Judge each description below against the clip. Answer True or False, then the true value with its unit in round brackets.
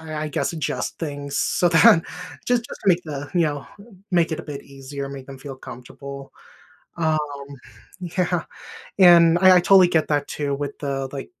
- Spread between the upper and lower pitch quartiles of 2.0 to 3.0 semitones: False (3.6 semitones)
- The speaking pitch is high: False (150 Hz)